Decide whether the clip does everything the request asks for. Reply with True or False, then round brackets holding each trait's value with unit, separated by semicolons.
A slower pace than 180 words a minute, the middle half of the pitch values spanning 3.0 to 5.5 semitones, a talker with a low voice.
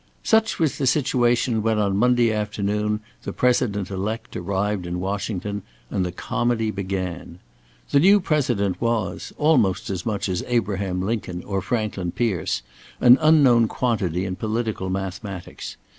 True (140 wpm; 4.0 semitones; 105 Hz)